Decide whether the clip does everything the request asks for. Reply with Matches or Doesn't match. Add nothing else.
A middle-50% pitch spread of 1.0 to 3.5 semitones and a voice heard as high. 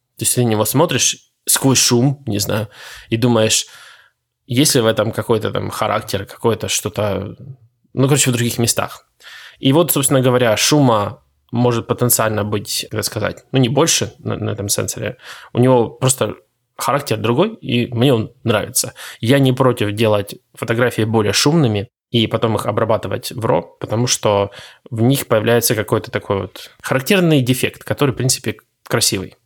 Doesn't match